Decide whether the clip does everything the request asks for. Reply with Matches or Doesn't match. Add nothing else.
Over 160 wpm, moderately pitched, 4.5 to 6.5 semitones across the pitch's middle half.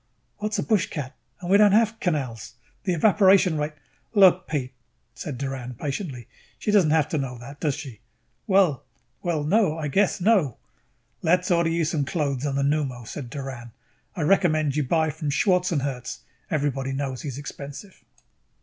Matches